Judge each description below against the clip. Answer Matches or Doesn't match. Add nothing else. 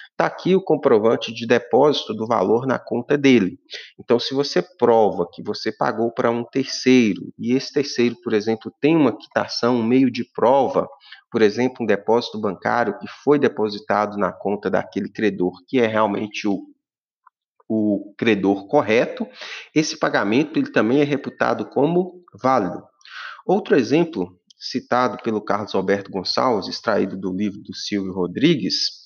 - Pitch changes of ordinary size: Matches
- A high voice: Doesn't match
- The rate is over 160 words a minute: Doesn't match